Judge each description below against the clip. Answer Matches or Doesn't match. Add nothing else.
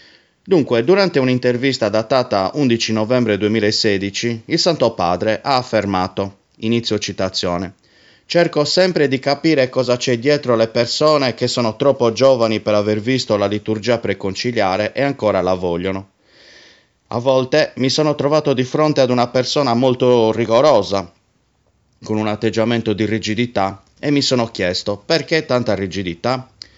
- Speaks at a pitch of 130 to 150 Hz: Doesn't match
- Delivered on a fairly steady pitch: Doesn't match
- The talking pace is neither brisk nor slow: Matches